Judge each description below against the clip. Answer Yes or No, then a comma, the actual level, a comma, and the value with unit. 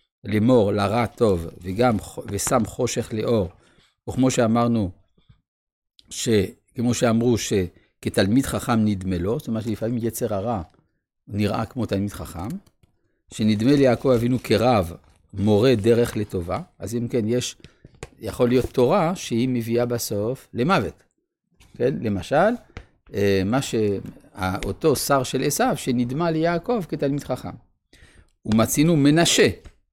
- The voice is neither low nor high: No, low, 115 Hz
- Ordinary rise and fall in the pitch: Yes, average, 3.9 semitones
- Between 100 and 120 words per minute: Yes, average, 110 wpm